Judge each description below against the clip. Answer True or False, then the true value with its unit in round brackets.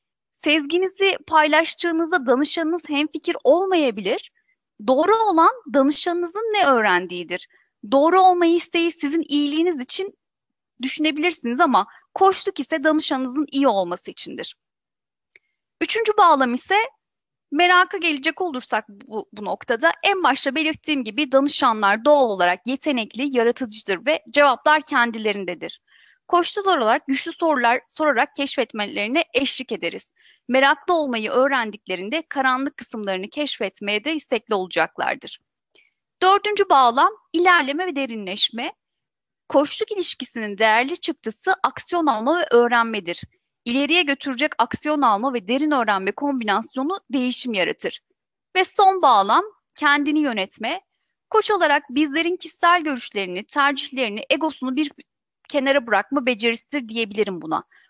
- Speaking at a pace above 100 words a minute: True (110 wpm)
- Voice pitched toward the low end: False (290 Hz)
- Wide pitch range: True (6.0 semitones)